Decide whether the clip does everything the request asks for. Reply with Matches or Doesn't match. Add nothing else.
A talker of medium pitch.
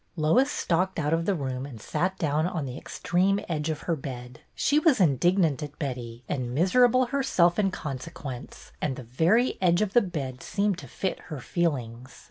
Matches